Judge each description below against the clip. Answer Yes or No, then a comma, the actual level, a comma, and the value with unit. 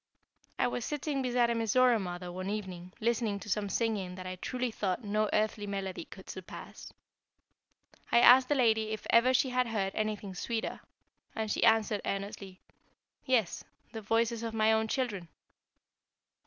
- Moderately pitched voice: No, high, 220 Hz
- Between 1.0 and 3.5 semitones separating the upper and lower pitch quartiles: Yes, average, 3.1 semitones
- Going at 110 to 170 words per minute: Yes, average, 160 wpm